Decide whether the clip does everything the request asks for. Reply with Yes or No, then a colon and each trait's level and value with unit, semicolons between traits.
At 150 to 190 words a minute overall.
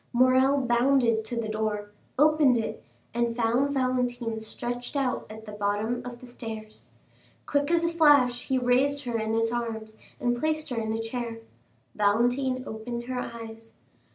Yes: average, 160 wpm